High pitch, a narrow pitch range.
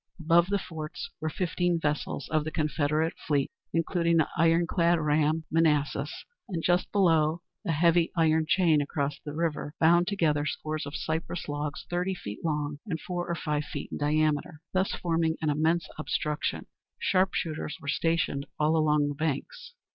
No: medium, 160 Hz; narrow, 2.1 semitones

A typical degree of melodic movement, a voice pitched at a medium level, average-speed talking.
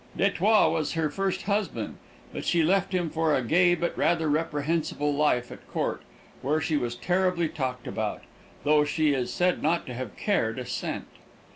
Yes: average, 3.4 semitones; medium, 160 Hz; average, 175 wpm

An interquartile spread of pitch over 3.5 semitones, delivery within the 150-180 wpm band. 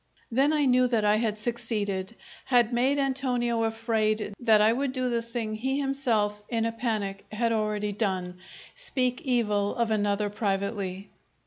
No: average, 3.0 semitones; average, 155 wpm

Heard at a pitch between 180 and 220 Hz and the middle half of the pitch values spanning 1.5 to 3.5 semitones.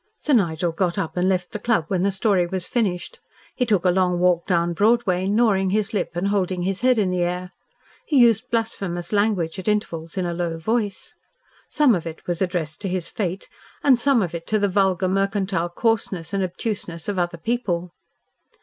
Yes: high, 190 Hz; average, 3.2 semitones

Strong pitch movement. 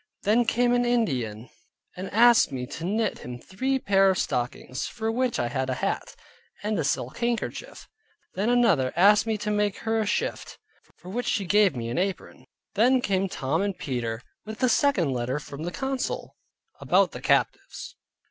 Yes: wide, 8.8 semitones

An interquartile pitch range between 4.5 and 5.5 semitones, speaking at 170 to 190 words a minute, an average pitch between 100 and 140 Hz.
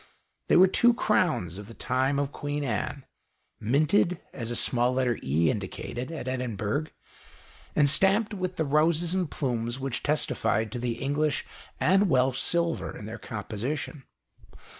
No: average, 5.2 semitones; average, 150 wpm; low, 135 Hz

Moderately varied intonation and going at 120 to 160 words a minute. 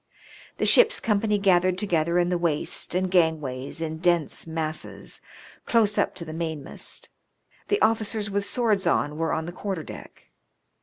Yes: average, 4.1 semitones; average, 155 wpm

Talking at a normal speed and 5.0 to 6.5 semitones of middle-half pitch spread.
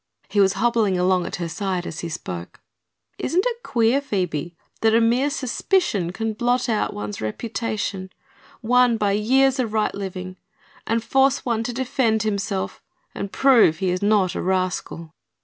No: average, 165 wpm; average, 4.6 semitones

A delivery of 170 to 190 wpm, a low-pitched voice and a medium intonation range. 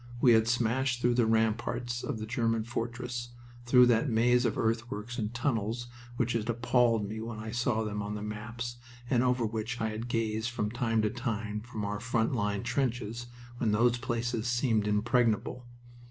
No: average, 180 wpm; low, 115 Hz; narrow, 1.8 semitones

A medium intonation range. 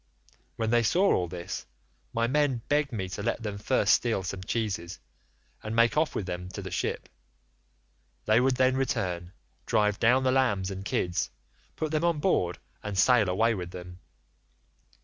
No: wide, 5.7 semitones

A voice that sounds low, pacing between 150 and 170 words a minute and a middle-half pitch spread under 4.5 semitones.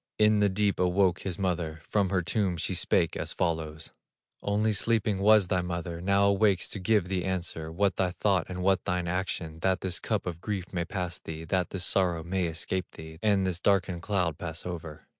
No: very low, 90 Hz; average, 200 wpm; narrow, 2.5 semitones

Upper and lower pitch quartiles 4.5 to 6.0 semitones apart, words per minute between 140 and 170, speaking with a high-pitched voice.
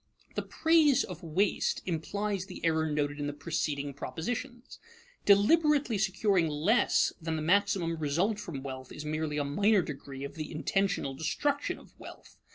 No: wide, 5.4 semitones; average, 155 wpm; medium, 165 Hz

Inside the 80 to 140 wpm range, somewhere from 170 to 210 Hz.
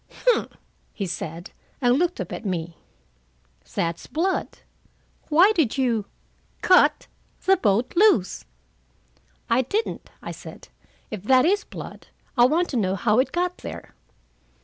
No: slow, 135 wpm; very high, 255 Hz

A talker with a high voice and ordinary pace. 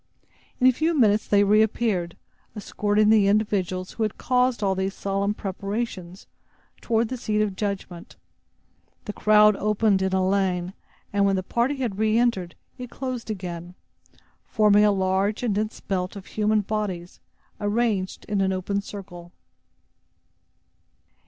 Yes: high, 205 Hz; average, 145 wpm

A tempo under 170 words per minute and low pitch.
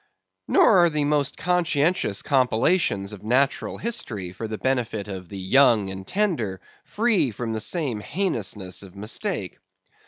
Yes: average, 145 wpm; low, 120 Hz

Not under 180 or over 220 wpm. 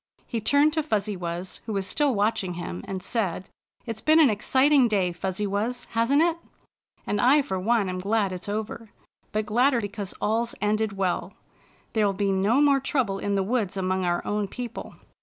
Yes: average, 190 wpm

